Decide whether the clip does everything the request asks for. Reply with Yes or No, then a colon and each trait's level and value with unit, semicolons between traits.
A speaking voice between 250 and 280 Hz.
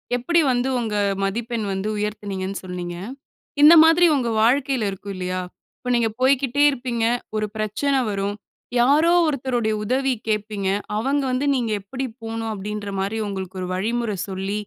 No: high, 225 Hz